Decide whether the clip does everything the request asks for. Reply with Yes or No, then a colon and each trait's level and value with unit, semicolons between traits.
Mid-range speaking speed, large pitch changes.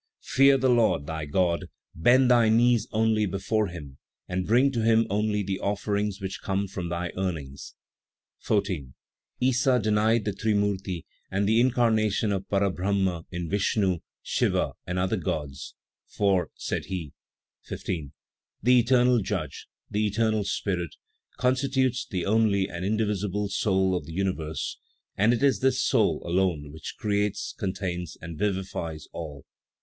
No: average, 145 wpm; average, 3.7 semitones